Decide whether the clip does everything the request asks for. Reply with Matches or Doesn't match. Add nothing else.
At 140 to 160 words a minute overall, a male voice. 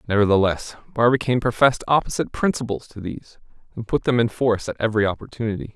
Matches